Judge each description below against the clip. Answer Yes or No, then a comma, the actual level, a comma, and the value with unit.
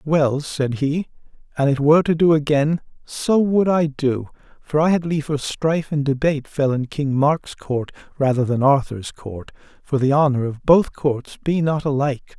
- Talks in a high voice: No, medium, 145 Hz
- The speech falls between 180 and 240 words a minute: Yes, average, 185 wpm